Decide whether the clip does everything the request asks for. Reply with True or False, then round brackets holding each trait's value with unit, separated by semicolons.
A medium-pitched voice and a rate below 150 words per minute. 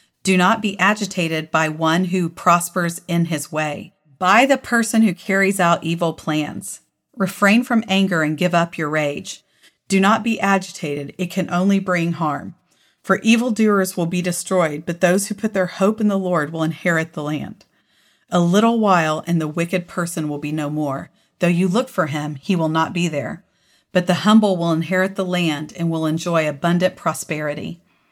False (175 Hz; 185 wpm)